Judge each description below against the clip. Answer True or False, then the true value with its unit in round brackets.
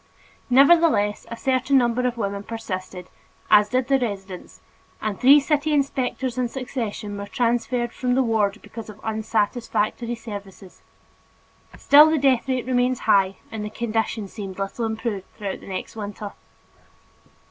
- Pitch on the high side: True (230 Hz)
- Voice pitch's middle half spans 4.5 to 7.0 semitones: False (3.7 semitones)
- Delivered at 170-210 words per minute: False (145 wpm)